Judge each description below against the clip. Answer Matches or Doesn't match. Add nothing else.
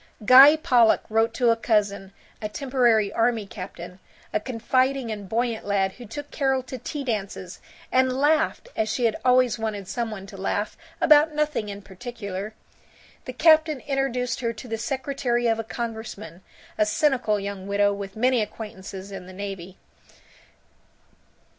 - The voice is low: Doesn't match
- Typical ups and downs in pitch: Matches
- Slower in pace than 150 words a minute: Doesn't match